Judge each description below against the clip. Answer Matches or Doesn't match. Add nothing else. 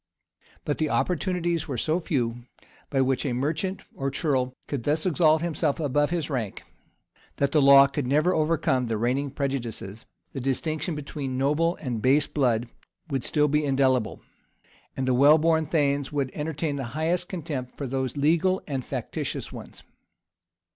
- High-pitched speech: Doesn't match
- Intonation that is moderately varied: Matches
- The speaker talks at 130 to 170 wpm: Matches